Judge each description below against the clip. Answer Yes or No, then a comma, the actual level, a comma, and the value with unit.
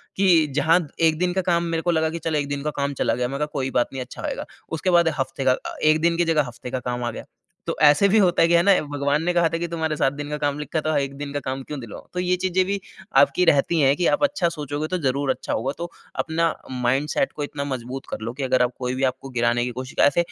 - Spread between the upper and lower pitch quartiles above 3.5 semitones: Yes, average, 3.9 semitones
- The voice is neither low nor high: Yes, medium, 145 Hz